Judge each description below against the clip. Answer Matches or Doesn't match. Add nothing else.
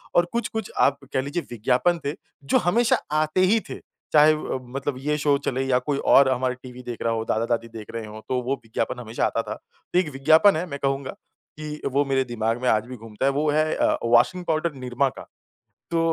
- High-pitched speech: Doesn't match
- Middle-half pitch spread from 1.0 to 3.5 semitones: Doesn't match